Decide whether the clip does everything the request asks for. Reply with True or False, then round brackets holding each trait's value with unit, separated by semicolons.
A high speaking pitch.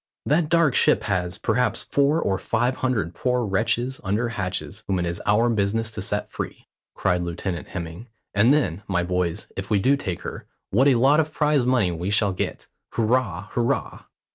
False (110 Hz)